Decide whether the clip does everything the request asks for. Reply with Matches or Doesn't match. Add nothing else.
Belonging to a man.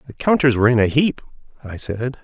Matches